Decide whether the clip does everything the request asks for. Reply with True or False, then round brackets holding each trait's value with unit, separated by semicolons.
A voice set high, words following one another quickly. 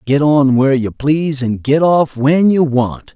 False (140 Hz; 210 wpm)